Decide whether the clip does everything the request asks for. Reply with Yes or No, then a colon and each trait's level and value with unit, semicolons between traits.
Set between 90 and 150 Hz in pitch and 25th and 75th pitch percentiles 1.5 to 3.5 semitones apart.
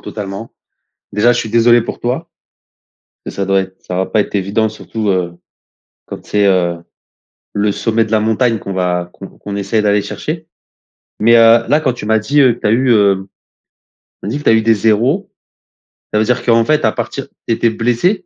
Yes: low, 110 Hz; average, 2.9 semitones